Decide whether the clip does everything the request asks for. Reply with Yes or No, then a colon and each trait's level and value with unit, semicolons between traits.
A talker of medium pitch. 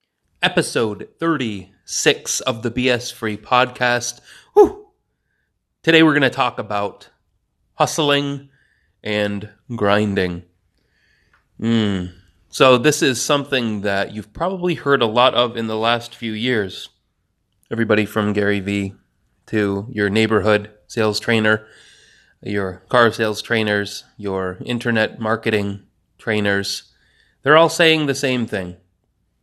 No: low, 110 Hz